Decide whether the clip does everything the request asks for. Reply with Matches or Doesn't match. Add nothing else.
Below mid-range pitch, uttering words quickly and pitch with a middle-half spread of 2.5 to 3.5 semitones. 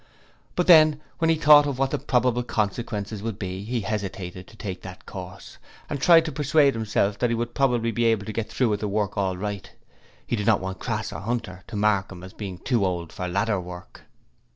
Doesn't match